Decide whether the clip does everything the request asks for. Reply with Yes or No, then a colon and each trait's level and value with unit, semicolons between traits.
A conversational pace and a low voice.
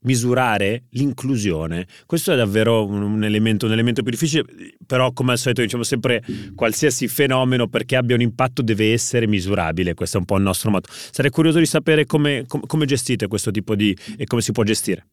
No: fast, 195 wpm; low, 120 Hz